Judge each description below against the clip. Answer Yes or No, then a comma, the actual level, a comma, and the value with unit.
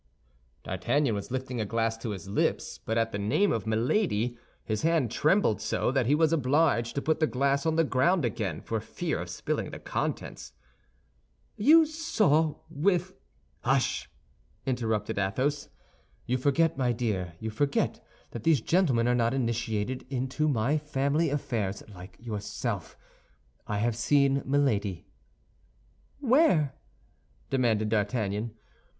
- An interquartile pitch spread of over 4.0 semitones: Yes, average, 5.2 semitones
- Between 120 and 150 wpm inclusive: Yes, average, 140 wpm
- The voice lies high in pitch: No, low, 125 Hz